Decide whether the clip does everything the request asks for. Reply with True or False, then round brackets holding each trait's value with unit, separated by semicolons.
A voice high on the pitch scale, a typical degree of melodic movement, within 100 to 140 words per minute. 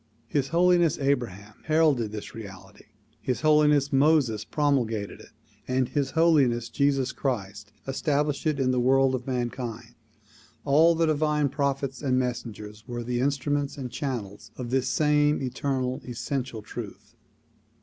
False (135 Hz; 3.3 semitones; 135 wpm)